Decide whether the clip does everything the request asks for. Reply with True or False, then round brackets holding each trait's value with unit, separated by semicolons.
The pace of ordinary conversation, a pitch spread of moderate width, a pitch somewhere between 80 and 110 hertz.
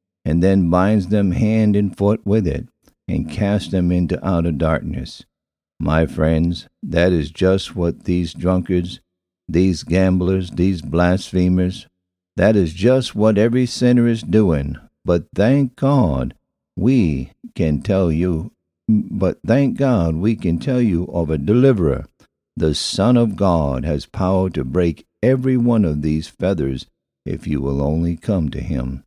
True (150 wpm; 4.5 semitones; 90 Hz)